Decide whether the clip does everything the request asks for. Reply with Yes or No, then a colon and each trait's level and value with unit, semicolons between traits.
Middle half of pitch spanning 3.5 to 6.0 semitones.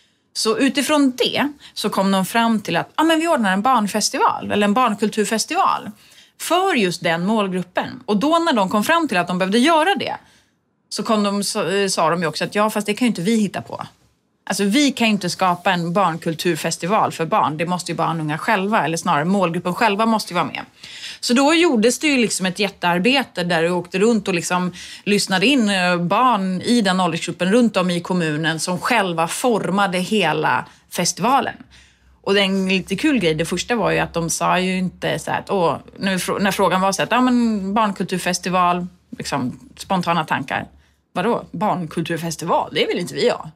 Yes: average, 4.2 semitones